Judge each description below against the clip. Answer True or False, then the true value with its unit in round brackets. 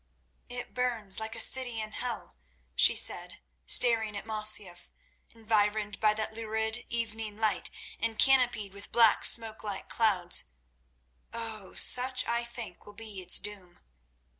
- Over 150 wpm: False (140 wpm)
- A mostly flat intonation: True (1.9 semitones)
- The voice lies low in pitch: False (220 Hz)